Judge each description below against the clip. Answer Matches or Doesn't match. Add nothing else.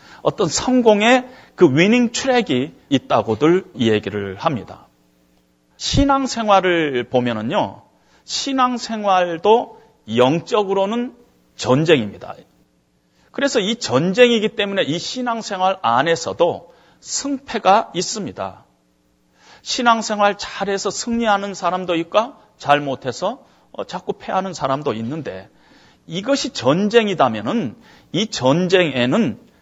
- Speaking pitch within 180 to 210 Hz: Matches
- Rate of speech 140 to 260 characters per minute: Matches